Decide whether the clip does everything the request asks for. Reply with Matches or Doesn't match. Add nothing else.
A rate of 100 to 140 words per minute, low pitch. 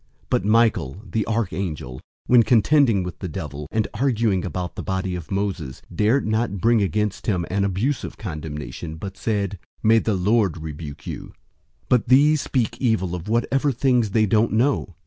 Doesn't match